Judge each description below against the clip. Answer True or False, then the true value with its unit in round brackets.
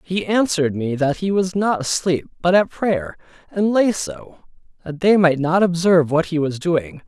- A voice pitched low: False (170 Hz)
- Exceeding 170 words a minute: True (195 wpm)